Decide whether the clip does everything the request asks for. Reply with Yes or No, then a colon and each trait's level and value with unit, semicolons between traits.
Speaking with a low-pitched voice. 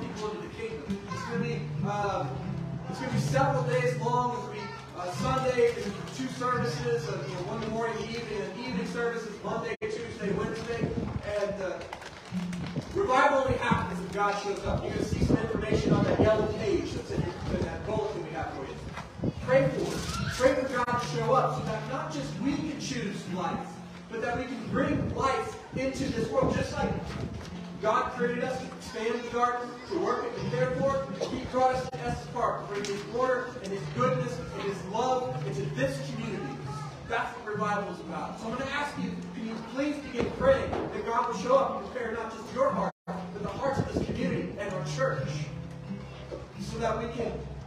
No: high, 210 Hz